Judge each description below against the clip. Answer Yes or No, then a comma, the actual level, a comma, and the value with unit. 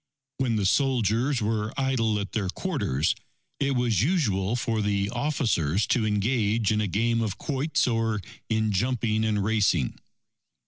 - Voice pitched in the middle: No, low, 110 Hz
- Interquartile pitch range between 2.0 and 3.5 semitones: Yes, average, 3.0 semitones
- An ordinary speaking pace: Yes, average, 145 wpm